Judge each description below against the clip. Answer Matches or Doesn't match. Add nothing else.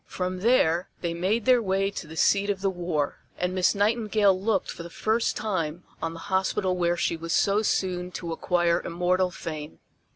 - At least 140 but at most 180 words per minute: Doesn't match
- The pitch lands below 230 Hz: Matches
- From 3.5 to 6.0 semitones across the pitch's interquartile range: Doesn't match